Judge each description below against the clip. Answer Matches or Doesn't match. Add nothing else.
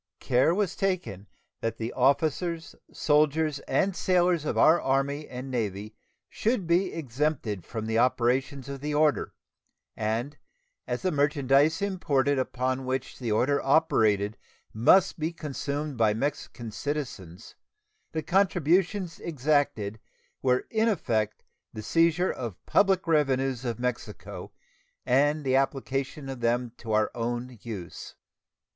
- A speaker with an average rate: Doesn't match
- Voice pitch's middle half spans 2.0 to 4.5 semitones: Doesn't match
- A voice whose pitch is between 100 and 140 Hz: Matches